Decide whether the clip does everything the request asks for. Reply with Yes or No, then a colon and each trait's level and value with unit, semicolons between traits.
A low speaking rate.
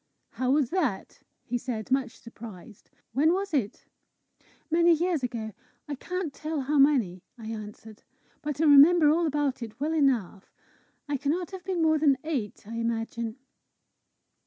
No: average, 155 wpm